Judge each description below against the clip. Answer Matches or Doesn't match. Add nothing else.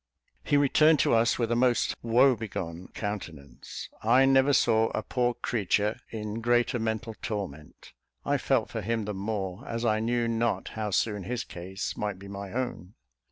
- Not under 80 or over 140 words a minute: Doesn't match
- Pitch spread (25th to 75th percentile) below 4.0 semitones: Matches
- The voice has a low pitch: Matches